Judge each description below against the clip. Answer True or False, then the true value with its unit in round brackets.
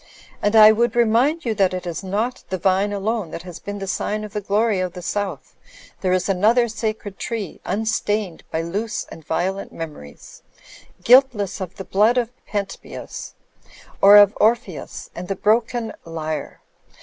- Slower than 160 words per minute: False (170 wpm)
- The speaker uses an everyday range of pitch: True (3.2 semitones)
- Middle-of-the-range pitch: False (205 Hz)